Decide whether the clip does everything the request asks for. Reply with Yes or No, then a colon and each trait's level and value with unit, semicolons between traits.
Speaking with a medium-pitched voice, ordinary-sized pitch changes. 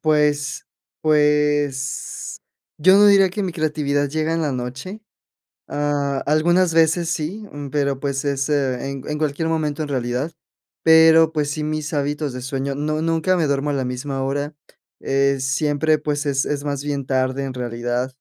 No: medium, 145 Hz; narrow, 2.3 semitones